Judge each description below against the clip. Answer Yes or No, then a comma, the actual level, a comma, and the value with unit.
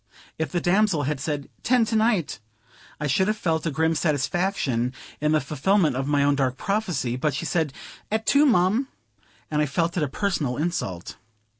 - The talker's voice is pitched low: No, medium, 160 Hz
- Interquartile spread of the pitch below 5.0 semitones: No, average, 5.3 semitones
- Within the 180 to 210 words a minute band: Yes, average, 185 wpm